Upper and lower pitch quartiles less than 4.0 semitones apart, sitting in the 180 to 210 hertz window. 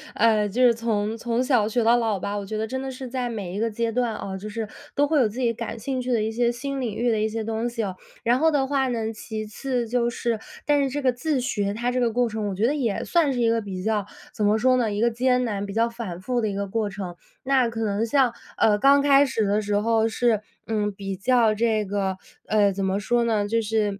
No: average, 2.9 semitones; high, 225 Hz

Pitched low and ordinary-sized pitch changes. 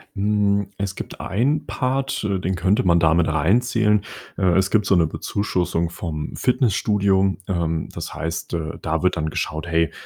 Yes: very low, 95 Hz; average, 3.9 semitones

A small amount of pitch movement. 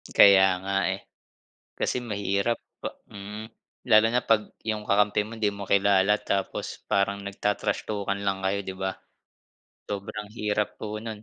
Yes: narrow, 1.2 semitones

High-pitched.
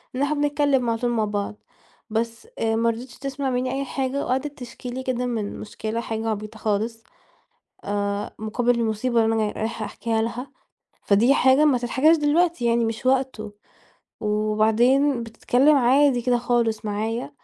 Yes: high, 235 Hz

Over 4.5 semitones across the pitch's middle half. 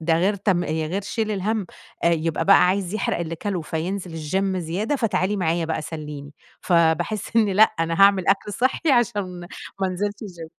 No: average, 3.7 semitones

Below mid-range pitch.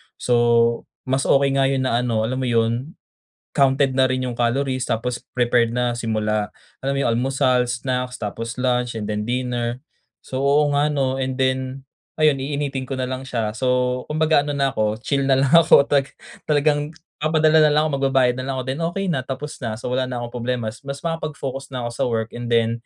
Yes: low, 130 Hz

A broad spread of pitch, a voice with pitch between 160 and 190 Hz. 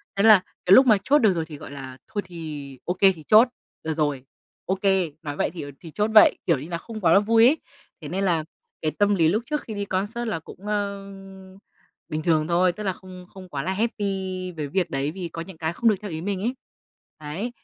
No: average, 4.4 semitones; medium, 185 Hz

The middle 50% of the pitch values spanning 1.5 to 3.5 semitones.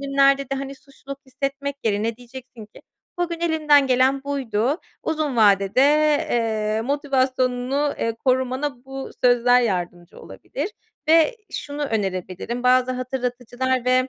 Yes: average, 2.7 semitones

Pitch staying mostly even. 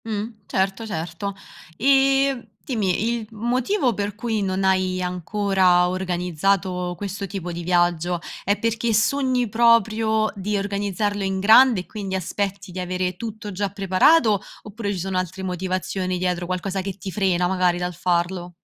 No: average, 3.0 semitones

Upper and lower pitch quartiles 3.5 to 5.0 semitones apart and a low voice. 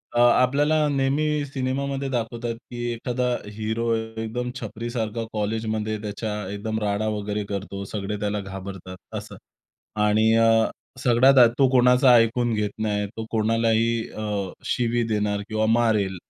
No: narrow, 2.5 semitones; low, 115 Hz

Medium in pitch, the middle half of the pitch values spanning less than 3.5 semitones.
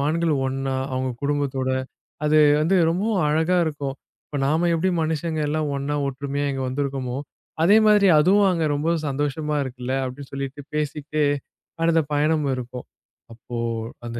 Yes: medium, 145 Hz; average, 2.9 semitones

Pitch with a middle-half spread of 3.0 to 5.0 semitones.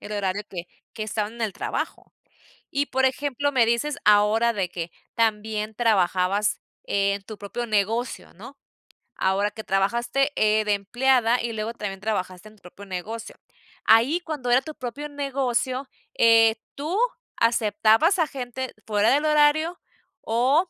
Yes: average, 4.2 semitones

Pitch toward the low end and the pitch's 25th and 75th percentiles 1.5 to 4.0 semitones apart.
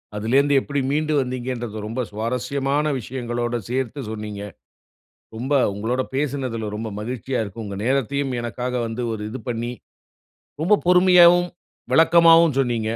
Yes: low, 125 Hz; average, 3.7 semitones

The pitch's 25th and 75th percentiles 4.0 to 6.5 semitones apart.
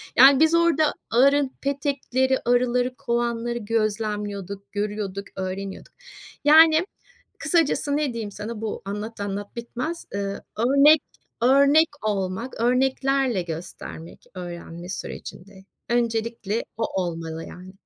Yes: average, 5.2 semitones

